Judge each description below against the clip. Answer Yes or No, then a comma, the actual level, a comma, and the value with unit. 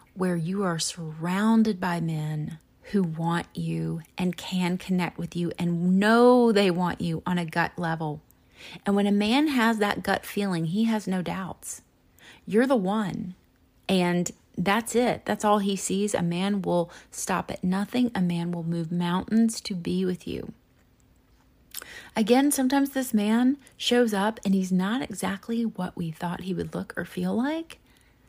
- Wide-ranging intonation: No, average, 4.2 semitones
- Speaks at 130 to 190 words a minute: Yes, average, 170 wpm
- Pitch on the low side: No, high, 190 Hz